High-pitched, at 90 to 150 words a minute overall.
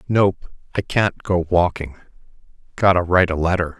No: very low, 90 Hz; average, 140 wpm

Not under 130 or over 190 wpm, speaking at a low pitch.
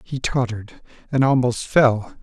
Yes: slow, 135 wpm; low, 125 Hz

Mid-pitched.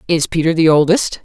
Yes: medium, 160 Hz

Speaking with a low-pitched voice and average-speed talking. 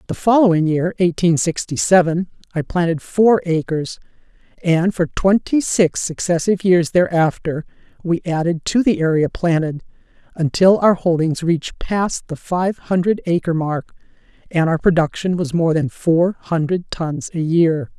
No: medium, 170 Hz; average, 145 wpm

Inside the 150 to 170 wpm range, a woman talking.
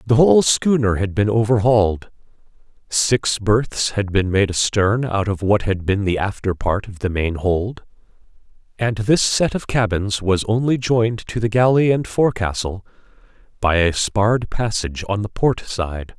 No: average, 165 wpm; male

